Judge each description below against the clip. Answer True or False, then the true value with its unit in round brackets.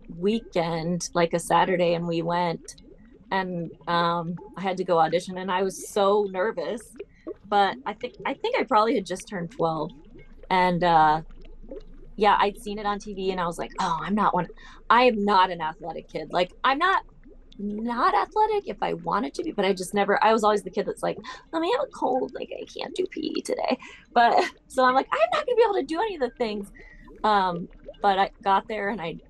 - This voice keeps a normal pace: False (215 wpm)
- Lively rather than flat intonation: True (5.8 semitones)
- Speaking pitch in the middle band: False (200 Hz)